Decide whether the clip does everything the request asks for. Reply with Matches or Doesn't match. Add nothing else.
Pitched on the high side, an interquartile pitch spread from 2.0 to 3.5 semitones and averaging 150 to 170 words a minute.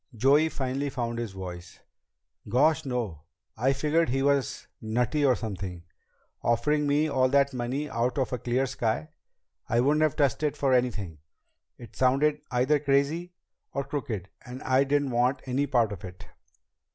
Doesn't match